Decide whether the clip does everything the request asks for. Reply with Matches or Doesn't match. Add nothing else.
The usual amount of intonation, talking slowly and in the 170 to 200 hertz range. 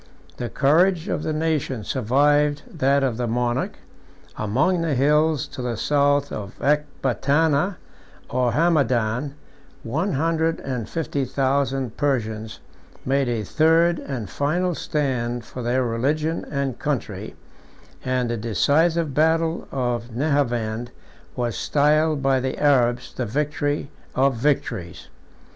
Doesn't match